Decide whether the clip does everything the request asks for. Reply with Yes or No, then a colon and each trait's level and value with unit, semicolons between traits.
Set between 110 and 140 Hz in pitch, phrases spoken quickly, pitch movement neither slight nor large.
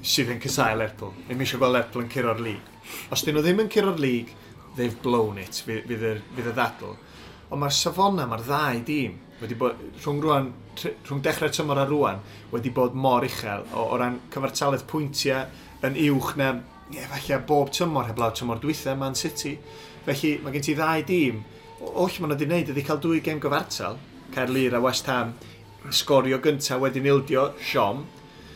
No: low, 135 Hz; average, 175 wpm; average, 4.0 semitones